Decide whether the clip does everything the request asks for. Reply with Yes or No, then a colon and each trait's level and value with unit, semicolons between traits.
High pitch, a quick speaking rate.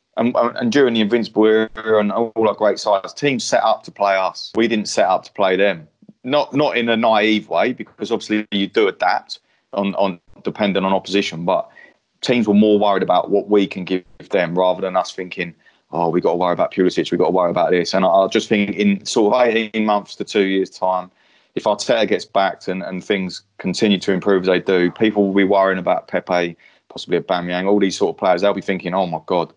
No: low, 100 Hz; fast, 235 wpm